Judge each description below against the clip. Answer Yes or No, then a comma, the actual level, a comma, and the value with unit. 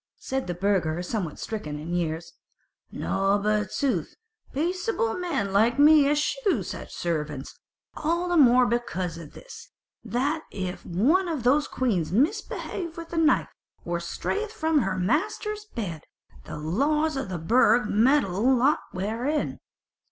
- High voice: Yes, high, 240 Hz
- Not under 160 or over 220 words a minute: No, average, 145 wpm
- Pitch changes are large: Yes, wide, 8.9 semitones